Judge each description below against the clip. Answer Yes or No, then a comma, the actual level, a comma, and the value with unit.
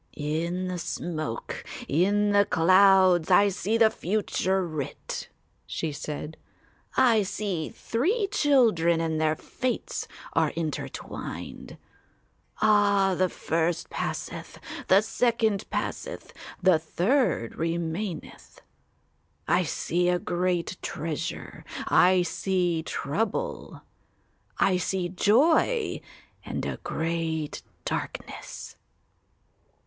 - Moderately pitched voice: Yes, medium, 180 Hz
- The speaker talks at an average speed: No, slow, 95 wpm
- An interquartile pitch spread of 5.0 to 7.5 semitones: No, average, 4.0 semitones